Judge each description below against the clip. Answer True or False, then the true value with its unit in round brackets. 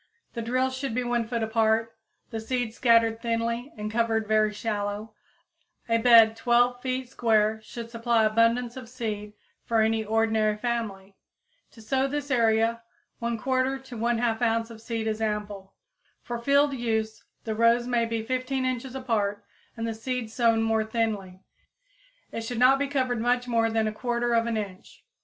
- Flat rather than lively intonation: True (1.8 semitones)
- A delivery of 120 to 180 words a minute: True (160 wpm)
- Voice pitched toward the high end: True (230 Hz)